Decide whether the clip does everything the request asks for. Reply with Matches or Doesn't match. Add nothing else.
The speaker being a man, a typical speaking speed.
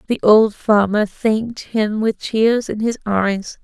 Doesn't match